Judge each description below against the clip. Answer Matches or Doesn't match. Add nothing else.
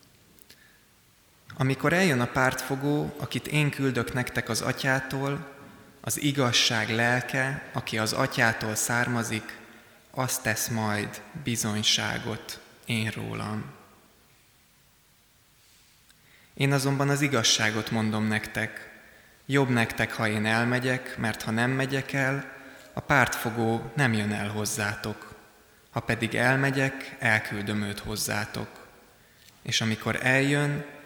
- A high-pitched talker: Doesn't match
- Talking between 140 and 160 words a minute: Doesn't match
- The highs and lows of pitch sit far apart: Doesn't match